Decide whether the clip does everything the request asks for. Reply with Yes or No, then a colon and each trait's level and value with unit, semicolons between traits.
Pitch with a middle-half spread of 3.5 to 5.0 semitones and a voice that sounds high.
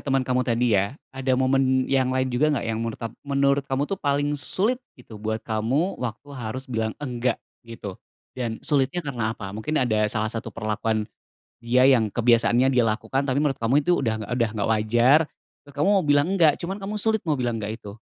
No: average, 3.8 semitones; low, 125 Hz